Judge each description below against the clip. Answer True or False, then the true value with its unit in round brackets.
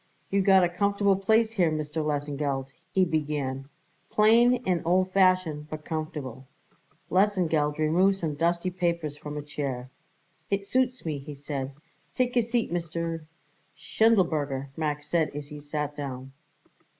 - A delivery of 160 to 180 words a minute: False (145 wpm)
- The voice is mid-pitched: True (160 Hz)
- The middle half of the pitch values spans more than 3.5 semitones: True (4.4 semitones)